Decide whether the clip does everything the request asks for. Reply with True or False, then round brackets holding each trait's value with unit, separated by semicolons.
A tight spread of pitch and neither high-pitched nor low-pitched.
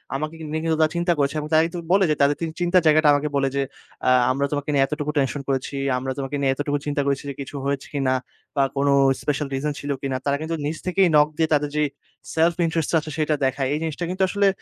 True (2.3 semitones; 150 Hz)